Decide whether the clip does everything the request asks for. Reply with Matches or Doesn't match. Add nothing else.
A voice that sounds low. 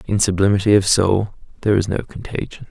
Matches